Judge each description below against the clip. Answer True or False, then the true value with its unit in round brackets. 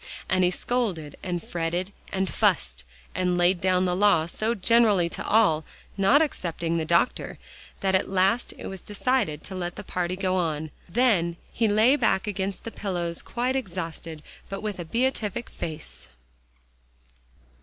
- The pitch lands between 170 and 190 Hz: True (185 Hz)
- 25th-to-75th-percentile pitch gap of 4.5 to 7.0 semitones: False (3.7 semitones)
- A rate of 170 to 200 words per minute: False (155 wpm)